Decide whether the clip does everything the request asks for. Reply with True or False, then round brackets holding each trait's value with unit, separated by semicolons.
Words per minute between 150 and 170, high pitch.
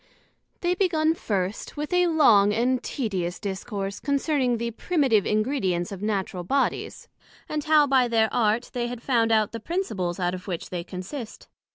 True (165 wpm; 230 Hz)